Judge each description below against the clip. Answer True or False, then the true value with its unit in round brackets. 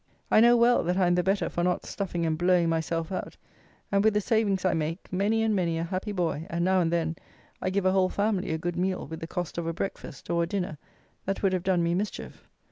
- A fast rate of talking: True (255 wpm)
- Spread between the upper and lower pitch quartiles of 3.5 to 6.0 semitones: False (2.7 semitones)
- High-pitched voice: False (180 Hz)